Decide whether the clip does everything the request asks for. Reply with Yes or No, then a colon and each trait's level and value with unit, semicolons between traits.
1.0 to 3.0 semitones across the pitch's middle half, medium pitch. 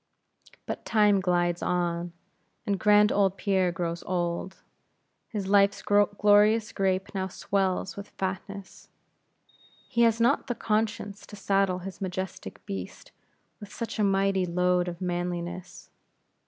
No: narrow, 2.4 semitones; high, 195 Hz